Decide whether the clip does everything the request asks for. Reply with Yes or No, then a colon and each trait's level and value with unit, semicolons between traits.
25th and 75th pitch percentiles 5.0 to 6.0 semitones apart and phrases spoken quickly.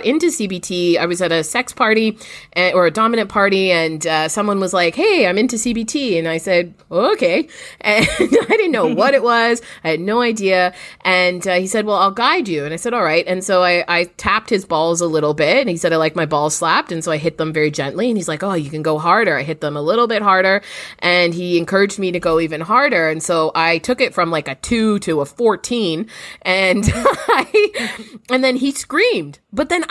Yes: wide, 5.6 semitones; fast, 240 wpm